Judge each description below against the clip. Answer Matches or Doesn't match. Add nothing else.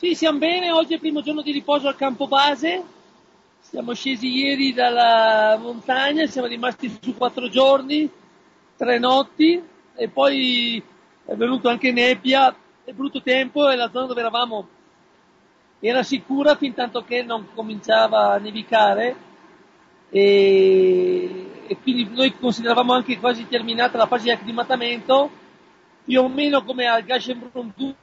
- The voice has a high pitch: Matches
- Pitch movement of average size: Matches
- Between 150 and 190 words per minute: Doesn't match